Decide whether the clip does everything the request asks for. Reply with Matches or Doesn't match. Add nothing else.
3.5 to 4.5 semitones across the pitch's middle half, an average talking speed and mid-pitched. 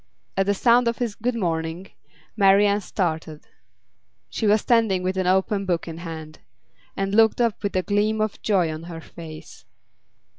Doesn't match